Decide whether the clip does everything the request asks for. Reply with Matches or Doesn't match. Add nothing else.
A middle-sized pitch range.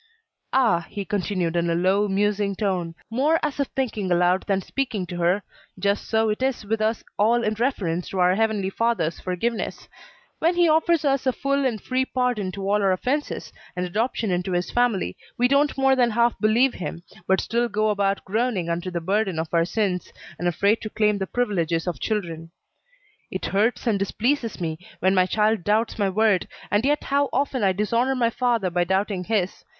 Matches